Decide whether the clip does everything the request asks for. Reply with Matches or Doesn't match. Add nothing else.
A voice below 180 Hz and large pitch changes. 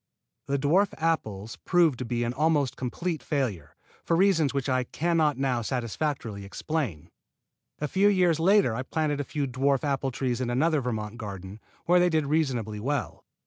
Doesn't match